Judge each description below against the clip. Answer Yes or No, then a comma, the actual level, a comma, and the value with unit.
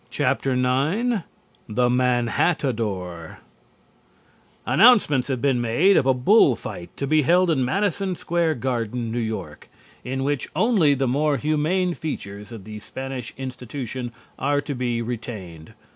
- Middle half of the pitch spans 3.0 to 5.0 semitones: Yes, average, 4.7 semitones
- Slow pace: Yes, slow, 130 wpm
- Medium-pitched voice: No, low, 130 Hz